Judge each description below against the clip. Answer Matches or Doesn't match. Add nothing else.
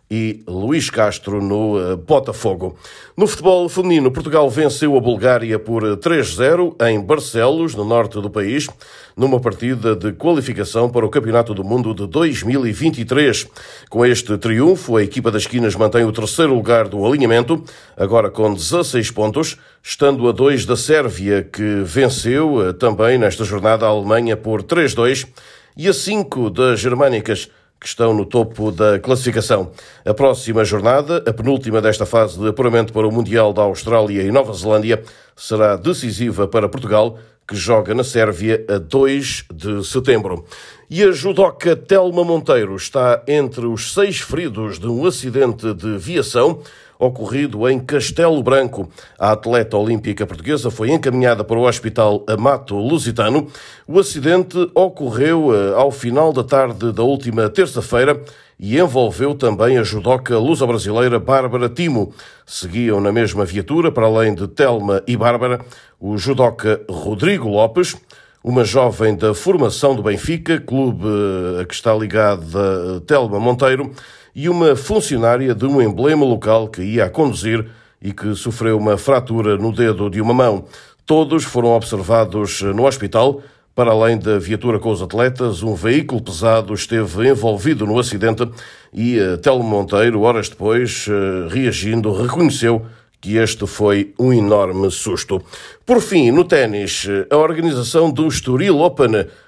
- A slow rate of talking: Doesn't match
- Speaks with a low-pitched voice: Matches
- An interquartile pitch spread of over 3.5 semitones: Matches